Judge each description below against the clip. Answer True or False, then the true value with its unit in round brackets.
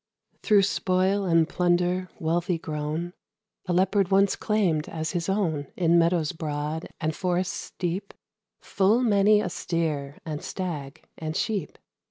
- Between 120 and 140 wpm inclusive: True (135 wpm)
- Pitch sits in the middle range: True (175 Hz)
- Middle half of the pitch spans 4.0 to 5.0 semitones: False (3.3 semitones)